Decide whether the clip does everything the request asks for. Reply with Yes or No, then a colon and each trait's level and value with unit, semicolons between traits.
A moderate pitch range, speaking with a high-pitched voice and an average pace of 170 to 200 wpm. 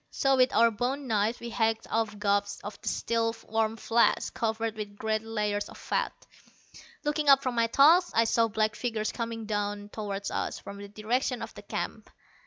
No: narrow, 2.0 semitones; high, 225 Hz; average, 185 wpm